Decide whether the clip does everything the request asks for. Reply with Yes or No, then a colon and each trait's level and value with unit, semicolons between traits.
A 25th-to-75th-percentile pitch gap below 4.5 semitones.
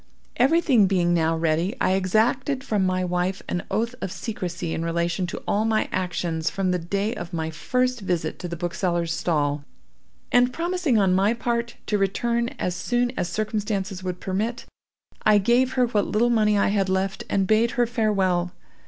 No: average, 4.8 semitones